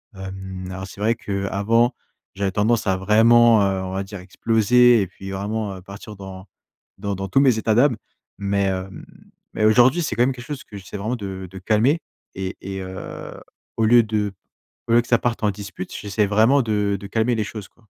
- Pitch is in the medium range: No, low, 105 Hz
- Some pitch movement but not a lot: Yes, average, 3.1 semitones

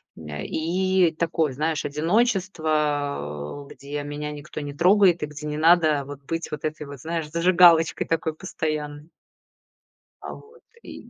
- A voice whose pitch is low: No, medium, 155 Hz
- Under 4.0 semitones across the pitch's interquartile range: Yes, narrow, 2.5 semitones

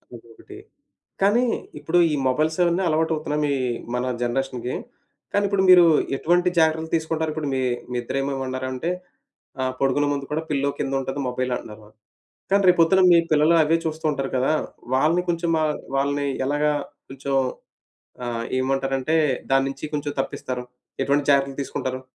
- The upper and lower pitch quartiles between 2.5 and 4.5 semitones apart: Yes, average, 3.2 semitones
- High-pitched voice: No, medium, 145 Hz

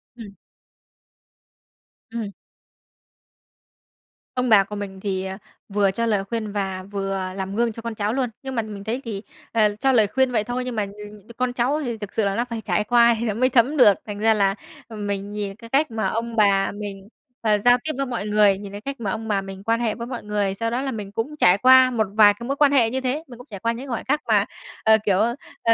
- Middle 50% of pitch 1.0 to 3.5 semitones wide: Yes, average, 3.1 semitones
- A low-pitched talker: No, high, 220 Hz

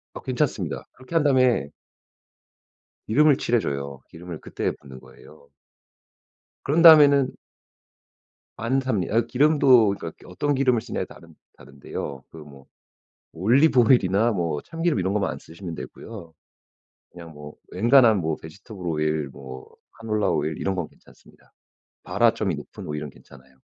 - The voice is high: No, low, 100 Hz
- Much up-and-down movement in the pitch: Yes, wide, 8.6 semitones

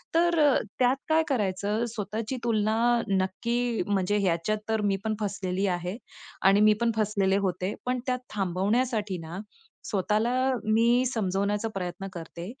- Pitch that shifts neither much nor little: Yes, average, 3.4 semitones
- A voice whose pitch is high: Yes, high, 210 Hz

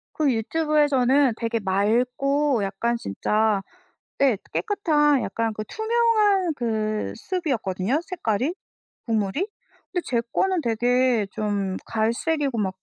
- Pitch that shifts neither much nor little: No, wide, 5.9 semitones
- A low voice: No, high, 245 Hz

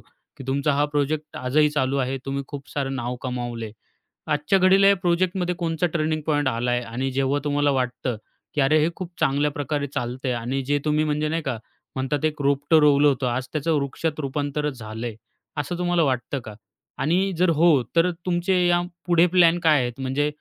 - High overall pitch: No, medium, 145 Hz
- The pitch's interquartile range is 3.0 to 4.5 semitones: Yes, average, 3.6 semitones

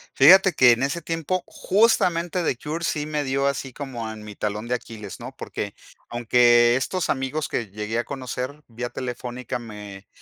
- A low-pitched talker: Yes, low, 130 Hz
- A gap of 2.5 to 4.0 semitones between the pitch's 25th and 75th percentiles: No, average, 4.4 semitones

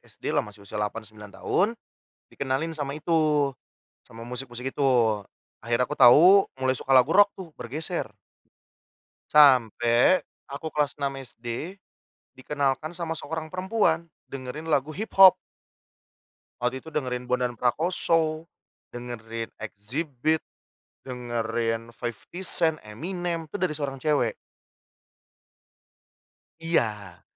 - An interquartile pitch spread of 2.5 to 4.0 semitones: No, average, 5.1 semitones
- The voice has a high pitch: No, medium, 140 Hz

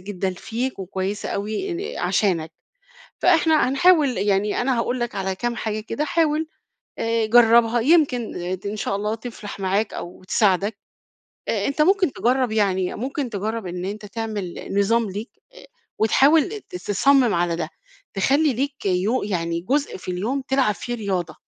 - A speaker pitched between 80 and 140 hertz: No, high, 225 Hz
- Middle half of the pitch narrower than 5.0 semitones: No, average, 5.3 semitones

